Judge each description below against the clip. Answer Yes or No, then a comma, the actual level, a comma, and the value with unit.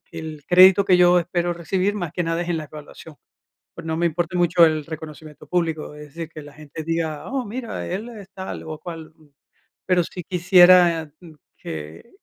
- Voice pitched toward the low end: No, medium, 170 Hz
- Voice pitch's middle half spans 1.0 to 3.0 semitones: Yes, narrow, 2.4 semitones